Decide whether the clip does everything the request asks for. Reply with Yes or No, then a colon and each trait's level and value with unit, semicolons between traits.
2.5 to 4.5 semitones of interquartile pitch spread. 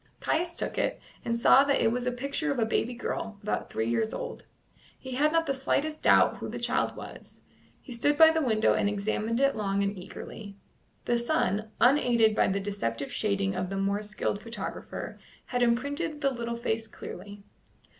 No: average, 5.2 semitones